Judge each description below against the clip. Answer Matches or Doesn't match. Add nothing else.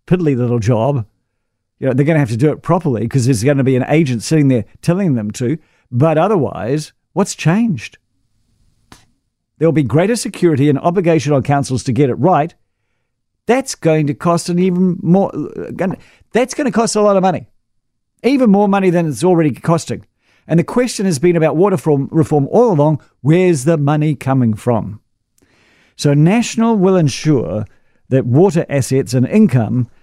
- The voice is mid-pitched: Matches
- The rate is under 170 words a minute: Doesn't match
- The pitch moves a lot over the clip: Matches